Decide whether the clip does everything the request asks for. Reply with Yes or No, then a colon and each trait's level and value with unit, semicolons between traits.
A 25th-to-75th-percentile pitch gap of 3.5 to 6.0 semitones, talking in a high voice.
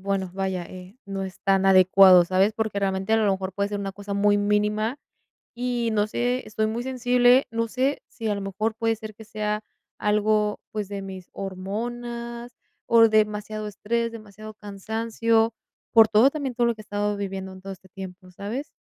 No: average, 2.7 semitones; high, 210 Hz